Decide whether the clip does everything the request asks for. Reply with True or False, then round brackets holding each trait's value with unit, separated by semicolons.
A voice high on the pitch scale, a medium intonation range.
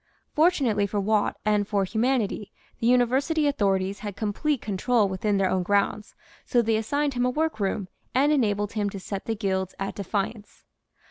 True (210 Hz; 3.8 semitones)